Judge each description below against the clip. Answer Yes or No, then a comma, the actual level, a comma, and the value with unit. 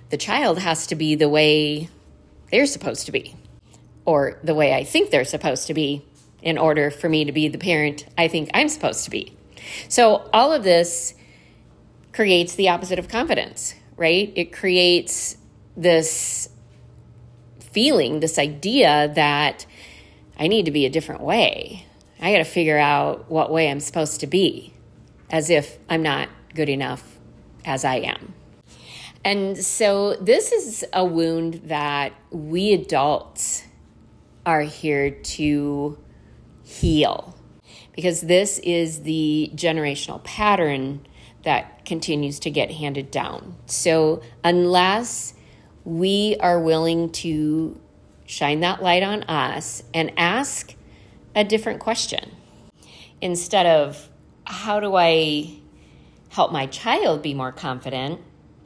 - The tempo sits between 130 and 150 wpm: Yes, slow, 135 wpm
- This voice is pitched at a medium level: Yes, medium, 160 Hz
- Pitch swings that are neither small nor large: Yes, average, 3.3 semitones